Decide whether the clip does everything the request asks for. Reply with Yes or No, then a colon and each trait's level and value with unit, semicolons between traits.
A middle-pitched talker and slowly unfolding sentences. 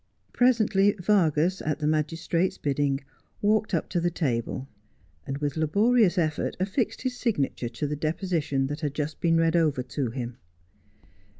No: medium, 155 Hz; average, 155 wpm